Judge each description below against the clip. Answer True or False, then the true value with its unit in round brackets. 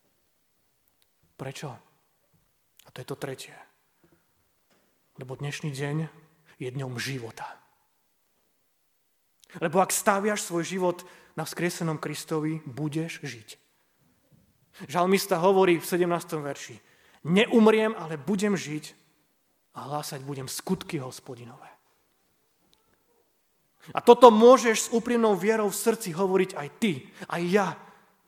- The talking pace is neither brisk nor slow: False (105 wpm)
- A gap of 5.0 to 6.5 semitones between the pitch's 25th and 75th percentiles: True (5.4 semitones)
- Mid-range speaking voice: True (170 Hz)